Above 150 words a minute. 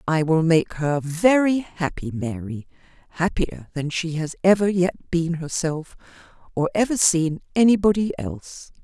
No: slow, 135 wpm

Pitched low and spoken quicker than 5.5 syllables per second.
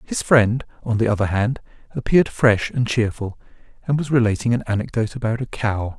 Yes: low, 115 Hz; 5.7 syllables/s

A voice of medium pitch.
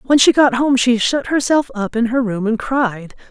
No: high, 245 Hz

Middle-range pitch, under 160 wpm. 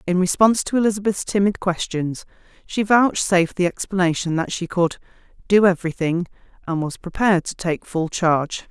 Yes: medium, 180 Hz; average, 150 wpm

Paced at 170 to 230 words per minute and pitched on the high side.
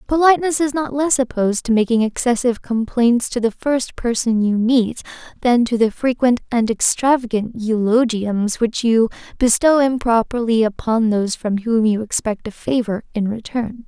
No: average, 155 wpm; high, 235 Hz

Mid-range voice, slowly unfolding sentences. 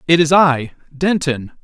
Yes: medium, 155 Hz; slow, 110 wpm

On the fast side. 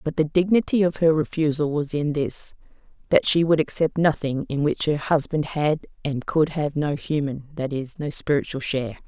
No: average, 185 wpm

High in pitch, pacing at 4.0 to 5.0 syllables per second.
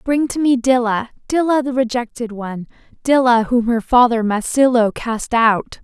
Yes: high, 240 Hz; 4.7 syllables/s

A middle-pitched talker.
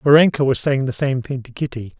No: low, 130 Hz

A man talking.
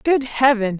No: female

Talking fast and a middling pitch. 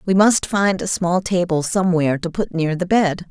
Yes: fast, 220 wpm; medium, 175 Hz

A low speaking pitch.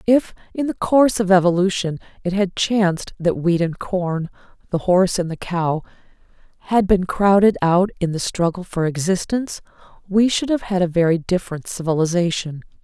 No: medium, 185 Hz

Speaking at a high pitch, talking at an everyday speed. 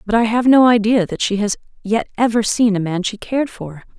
No: high, 220 Hz; fast, 240 wpm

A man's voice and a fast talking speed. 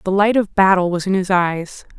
No: female; fast, 240 wpm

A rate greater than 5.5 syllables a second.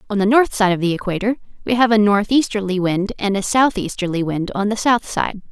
Yes: 5.7 syllables/s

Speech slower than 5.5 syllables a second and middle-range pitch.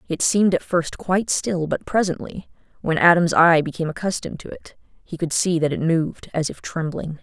No: 5.6 syllables/s; medium, 170 Hz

